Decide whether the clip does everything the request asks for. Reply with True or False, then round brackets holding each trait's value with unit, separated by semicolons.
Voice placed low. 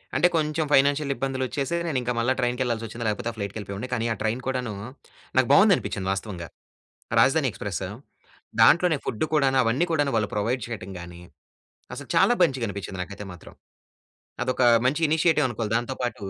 True (125 Hz)